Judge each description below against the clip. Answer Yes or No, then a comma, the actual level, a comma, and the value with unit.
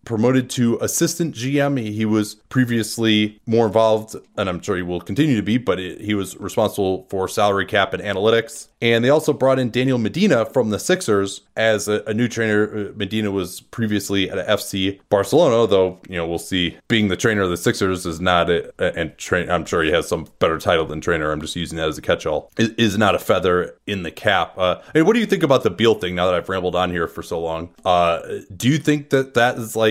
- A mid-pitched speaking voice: No, low, 105 Hz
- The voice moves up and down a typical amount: Yes, average, 4.2 semitones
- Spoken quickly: Yes, fast, 240 wpm